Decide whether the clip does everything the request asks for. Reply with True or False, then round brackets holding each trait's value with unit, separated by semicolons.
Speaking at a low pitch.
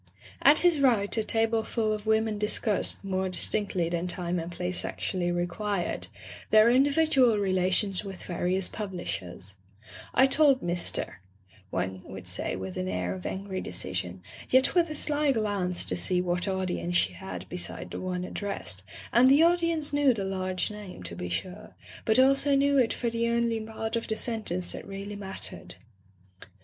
False (195 Hz)